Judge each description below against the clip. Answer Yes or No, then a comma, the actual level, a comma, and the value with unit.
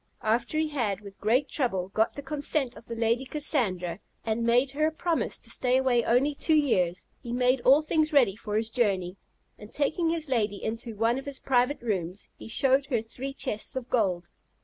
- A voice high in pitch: Yes, high, 245 Hz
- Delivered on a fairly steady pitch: No, average, 4.5 semitones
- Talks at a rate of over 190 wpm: Yes, average, 200 wpm